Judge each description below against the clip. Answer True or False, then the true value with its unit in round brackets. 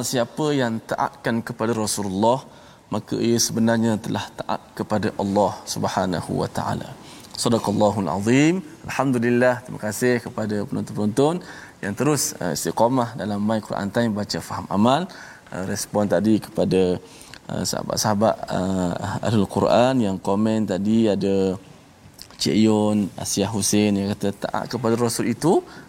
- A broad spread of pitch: False (2.8 semitones)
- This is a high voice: False (105 Hz)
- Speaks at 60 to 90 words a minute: False (120 wpm)